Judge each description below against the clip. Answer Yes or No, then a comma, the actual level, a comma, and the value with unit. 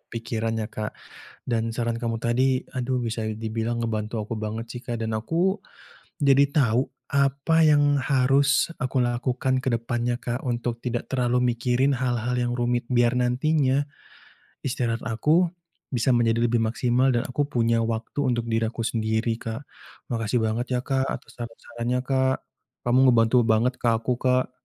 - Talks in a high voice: No, low, 120 Hz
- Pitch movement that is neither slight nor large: No, narrow, 1.9 semitones